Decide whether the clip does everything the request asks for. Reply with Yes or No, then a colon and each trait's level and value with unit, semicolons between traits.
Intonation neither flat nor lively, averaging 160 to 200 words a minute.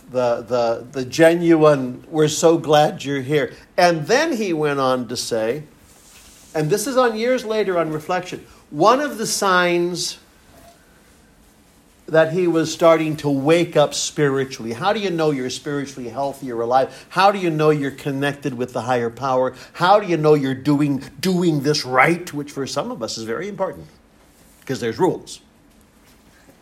Yes: average, 4.7 semitones; average, 170 wpm